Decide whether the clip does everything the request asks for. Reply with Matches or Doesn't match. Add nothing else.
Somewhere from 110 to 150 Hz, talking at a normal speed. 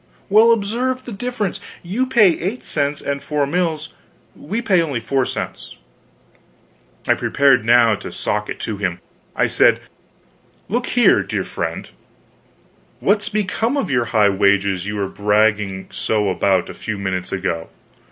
Matches